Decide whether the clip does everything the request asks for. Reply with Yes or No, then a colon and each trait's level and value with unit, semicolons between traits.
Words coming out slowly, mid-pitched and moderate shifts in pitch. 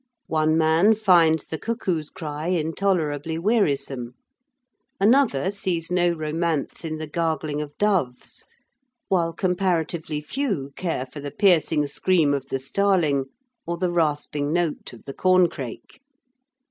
Yes: slow, 125 wpm; medium, 160 Hz; average, 3.7 semitones